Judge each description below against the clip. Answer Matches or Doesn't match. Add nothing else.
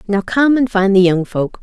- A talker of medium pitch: Doesn't match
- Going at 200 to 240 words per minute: Doesn't match